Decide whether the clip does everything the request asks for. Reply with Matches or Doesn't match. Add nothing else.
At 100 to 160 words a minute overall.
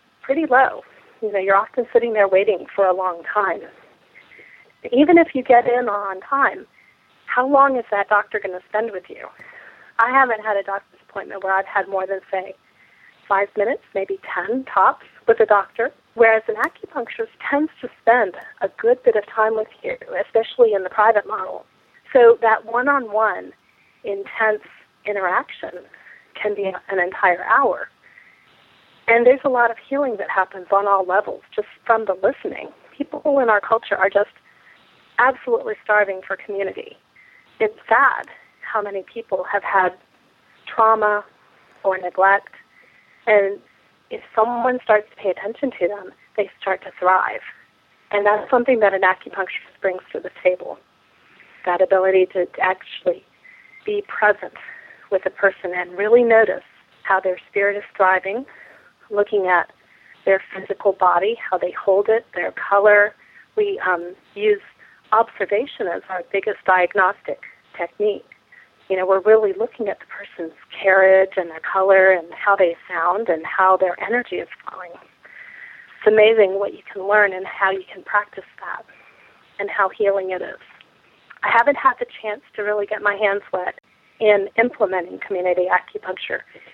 Matches